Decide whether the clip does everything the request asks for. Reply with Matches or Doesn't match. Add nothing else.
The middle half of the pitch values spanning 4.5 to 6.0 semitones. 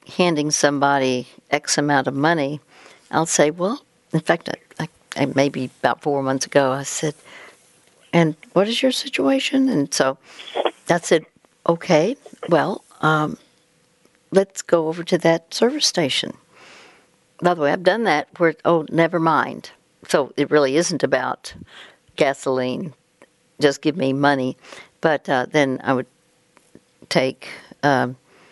Doesn't match